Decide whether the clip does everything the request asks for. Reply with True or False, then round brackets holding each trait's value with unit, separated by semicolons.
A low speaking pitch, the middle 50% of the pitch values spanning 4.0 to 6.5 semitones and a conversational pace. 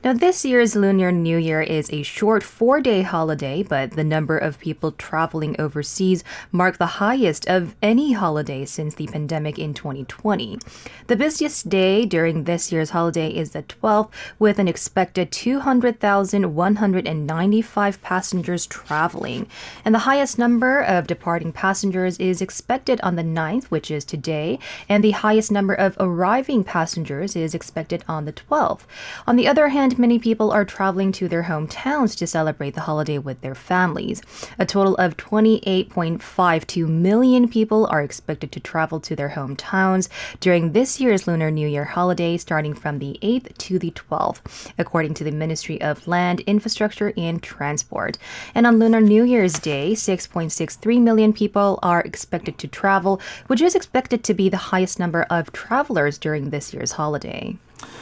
False (185 Hz; 5.1 semitones; 160 wpm)